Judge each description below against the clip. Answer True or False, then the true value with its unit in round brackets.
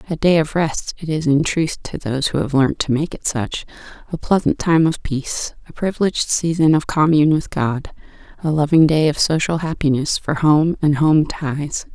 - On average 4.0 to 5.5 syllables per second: True (5.0 syllables/s)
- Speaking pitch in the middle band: True (150 Hz)